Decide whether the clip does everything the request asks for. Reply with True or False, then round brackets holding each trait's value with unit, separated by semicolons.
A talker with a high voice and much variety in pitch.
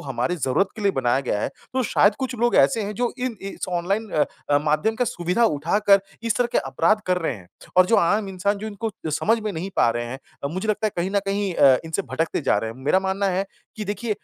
True (195 Hz; 5.7 semitones)